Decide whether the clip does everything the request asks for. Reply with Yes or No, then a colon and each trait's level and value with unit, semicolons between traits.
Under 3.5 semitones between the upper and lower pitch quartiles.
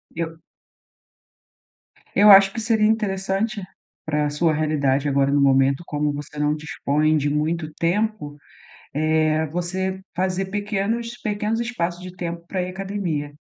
No: average, 4.7 semitones